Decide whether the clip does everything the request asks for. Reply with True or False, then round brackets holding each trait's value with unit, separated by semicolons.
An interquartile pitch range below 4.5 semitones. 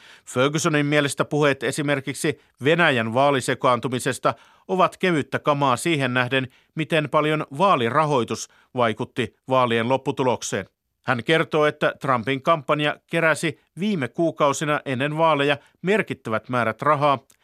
True (3.1 semitones)